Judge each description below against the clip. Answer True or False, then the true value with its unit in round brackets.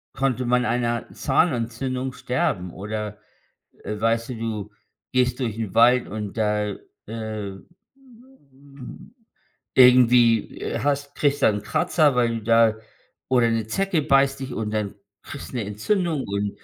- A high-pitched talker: False (115 Hz)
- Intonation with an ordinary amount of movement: True (3.4 semitones)